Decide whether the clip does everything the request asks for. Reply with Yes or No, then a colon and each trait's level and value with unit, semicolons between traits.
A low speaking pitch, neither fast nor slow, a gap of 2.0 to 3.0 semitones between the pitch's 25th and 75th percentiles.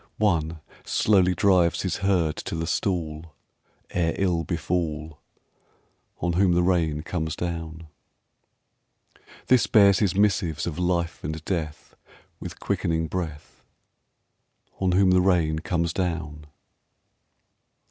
No: very low, 85 Hz; slow, 115 wpm; narrow, 2.4 semitones